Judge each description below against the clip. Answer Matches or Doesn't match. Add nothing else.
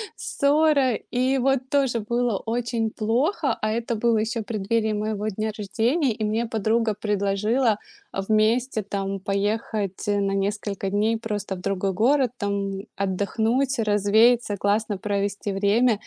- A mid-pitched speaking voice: Doesn't match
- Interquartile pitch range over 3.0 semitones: Doesn't match